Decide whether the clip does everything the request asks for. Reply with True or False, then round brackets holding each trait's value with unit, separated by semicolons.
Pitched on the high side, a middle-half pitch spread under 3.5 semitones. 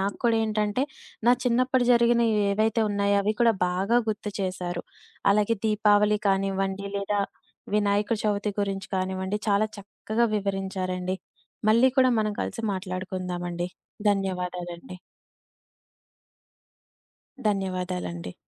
True (200 Hz; 2.5 semitones)